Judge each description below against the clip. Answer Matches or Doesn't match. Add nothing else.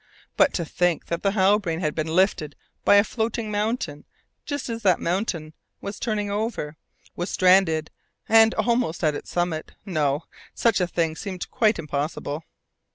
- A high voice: Doesn't match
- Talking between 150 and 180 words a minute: Matches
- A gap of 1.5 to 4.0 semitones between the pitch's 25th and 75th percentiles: Doesn't match